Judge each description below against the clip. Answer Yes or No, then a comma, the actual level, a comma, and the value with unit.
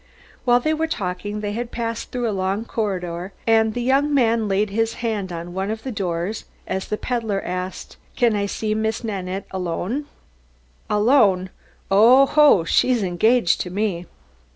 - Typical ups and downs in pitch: Yes, average, 3.8 semitones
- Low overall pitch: No, high, 215 Hz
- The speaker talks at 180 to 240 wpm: No, average, 160 wpm